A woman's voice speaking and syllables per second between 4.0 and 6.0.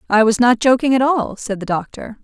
Yes: female; 5.5 syllables/s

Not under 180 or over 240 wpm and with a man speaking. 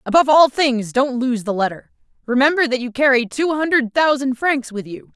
No: average, 200 wpm; female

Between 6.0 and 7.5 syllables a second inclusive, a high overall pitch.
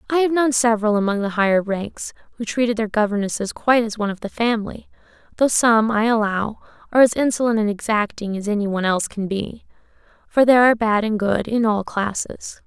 Yes: 6.1 syllables/s; high, 220 Hz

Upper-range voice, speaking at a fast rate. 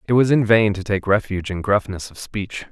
No: low, 100 Hz; fast, 245 wpm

